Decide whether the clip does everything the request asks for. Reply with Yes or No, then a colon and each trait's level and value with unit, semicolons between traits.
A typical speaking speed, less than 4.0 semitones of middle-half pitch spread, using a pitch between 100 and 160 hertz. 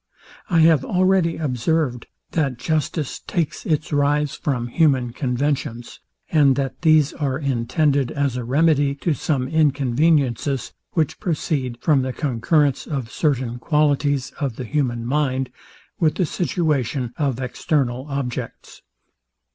No: slow, 125 wpm; average, 3.4 semitones; medium, 140 Hz